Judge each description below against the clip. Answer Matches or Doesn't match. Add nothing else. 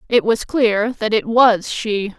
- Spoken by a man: Doesn't match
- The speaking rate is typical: Matches